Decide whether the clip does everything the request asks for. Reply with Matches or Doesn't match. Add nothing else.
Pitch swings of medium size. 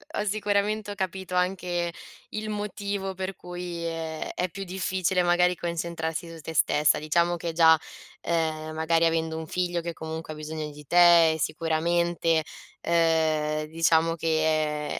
Doesn't match